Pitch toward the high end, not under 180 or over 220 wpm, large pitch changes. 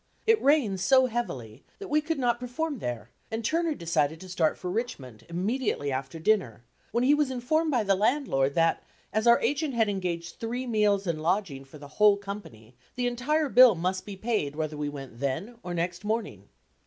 Yes: high, 205 Hz; average, 190 wpm; wide, 7.7 semitones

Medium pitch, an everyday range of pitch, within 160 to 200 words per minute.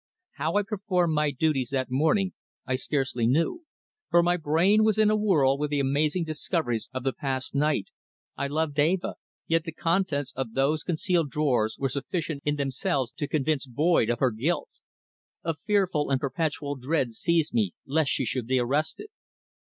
Yes: medium, 150 Hz; average, 3.9 semitones; average, 175 wpm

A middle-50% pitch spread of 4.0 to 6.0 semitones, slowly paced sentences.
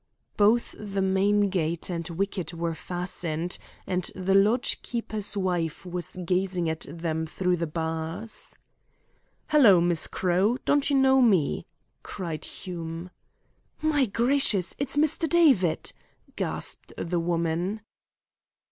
Yes: average, 4.3 semitones; slow, 120 wpm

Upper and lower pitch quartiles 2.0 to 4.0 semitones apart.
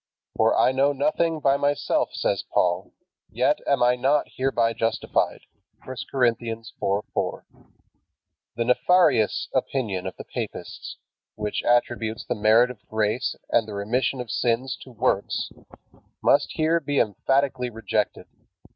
Yes: average, 3.5 semitones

